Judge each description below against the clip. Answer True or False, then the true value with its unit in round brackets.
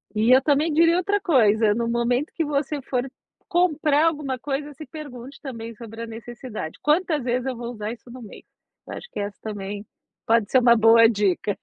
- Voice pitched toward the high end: True (245 Hz)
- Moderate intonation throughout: True (4.7 semitones)